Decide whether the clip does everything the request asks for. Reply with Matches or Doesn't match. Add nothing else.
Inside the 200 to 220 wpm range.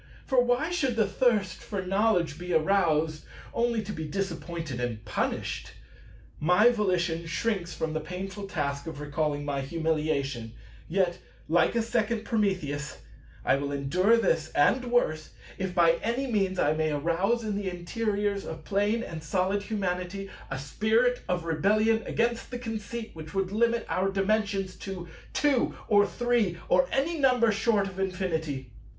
Doesn't match